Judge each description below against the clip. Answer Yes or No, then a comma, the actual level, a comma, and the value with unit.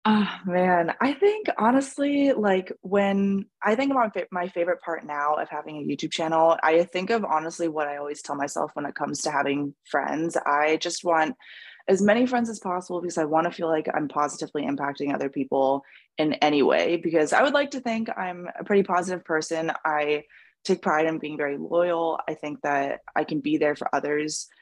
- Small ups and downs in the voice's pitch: No, average, 4.1 semitones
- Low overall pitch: No, medium, 165 Hz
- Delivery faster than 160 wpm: Yes, average, 200 wpm